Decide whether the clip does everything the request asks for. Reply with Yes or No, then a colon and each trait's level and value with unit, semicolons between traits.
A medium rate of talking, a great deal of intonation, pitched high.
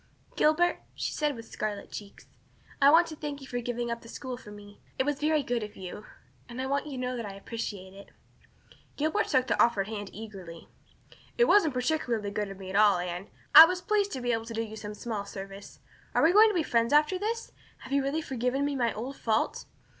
No: fast, 230 wpm; wide, 6.0 semitones; high, 245 Hz